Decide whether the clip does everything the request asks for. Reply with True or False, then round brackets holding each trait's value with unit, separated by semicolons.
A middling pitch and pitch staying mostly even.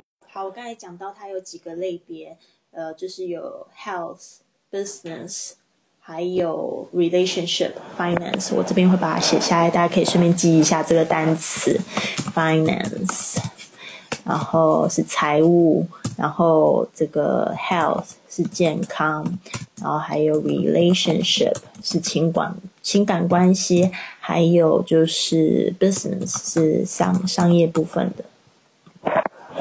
True (175 Hz; 2.3 semitones)